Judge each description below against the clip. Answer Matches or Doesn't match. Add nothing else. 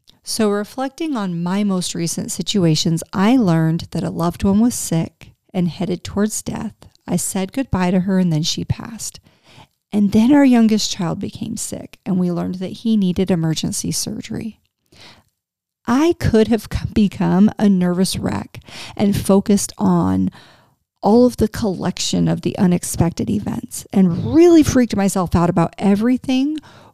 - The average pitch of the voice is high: Matches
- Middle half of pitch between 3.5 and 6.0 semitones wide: Matches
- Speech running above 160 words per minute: Doesn't match